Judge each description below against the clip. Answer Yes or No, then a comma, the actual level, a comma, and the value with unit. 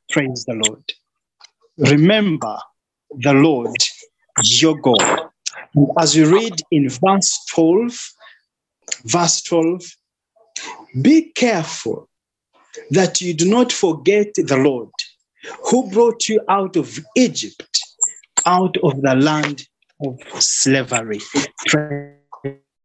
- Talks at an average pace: No, slow, 100 wpm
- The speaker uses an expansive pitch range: Yes, wide, 7.5 semitones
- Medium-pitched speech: Yes, medium, 165 Hz